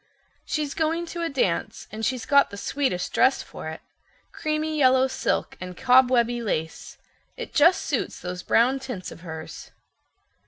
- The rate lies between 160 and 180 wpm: No, average, 150 wpm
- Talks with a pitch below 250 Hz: No, very high, 255 Hz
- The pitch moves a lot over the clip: Yes, wide, 7.6 semitones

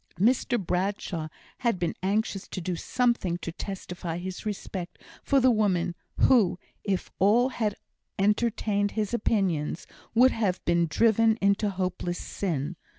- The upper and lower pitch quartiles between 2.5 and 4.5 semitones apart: Yes, average, 3.8 semitones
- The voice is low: No, high, 195 Hz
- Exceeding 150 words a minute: No, slow, 135 wpm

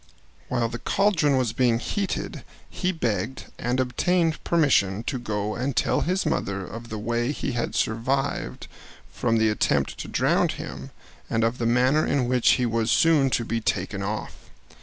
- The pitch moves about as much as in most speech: Yes, average, 3.6 semitones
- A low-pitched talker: Yes, low, 120 Hz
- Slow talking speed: No, average, 170 wpm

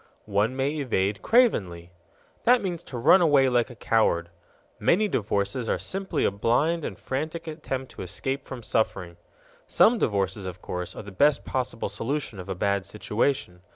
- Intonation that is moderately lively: No, wide, 7.0 semitones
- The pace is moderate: Yes, average, 165 wpm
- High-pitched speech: No, low, 120 Hz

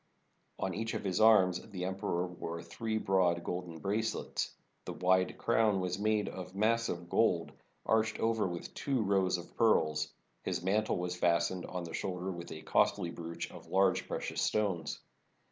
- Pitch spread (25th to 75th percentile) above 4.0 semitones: No, average, 3.6 semitones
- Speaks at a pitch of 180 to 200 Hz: No, very low, 95 Hz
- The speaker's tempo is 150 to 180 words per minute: Yes, average, 160 wpm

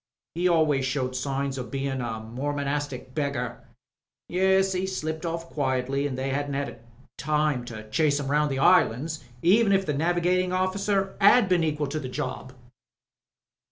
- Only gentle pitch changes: No, average, 4.7 semitones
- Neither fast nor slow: Yes, average, 155 wpm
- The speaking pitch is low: No, medium, 145 Hz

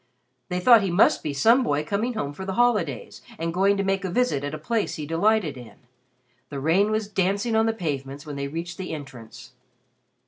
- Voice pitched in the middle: Yes, medium, 180 Hz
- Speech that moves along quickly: Yes, fast, 210 wpm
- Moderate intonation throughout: No, wide, 6.5 semitones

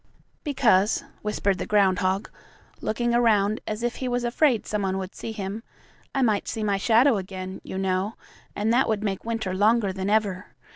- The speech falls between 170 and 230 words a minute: Yes, average, 180 wpm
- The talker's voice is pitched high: Yes, high, 210 Hz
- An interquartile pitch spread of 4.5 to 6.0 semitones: No, average, 3.2 semitones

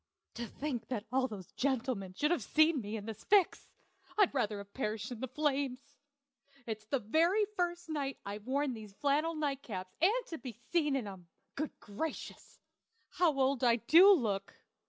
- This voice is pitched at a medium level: No, very high, 265 Hz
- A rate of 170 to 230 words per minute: Yes, average, 175 wpm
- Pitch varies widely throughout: Yes, wide, 6.1 semitones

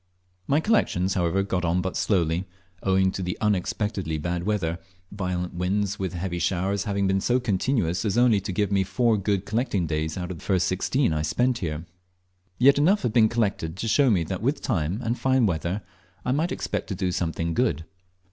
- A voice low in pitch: Yes, very low, 95 Hz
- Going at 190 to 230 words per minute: Yes, average, 195 wpm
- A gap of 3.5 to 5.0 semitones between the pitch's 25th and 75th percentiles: Yes, average, 3.9 semitones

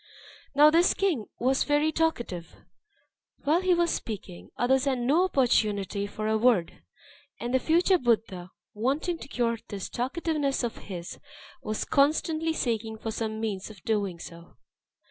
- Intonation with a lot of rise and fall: Yes, wide, 6.1 semitones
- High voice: Yes, high, 240 Hz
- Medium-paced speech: Yes, average, 145 wpm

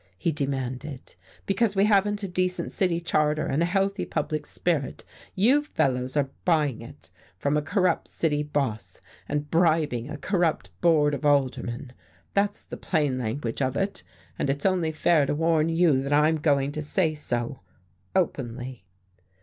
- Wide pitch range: No, average, 4.3 semitones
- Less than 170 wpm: Yes, average, 155 wpm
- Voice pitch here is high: No, medium, 150 Hz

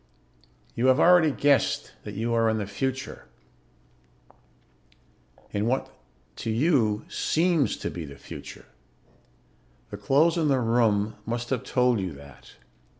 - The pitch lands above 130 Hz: No, low, 120 Hz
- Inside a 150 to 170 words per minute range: No, slow, 135 wpm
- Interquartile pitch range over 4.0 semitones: Yes, average, 4.7 semitones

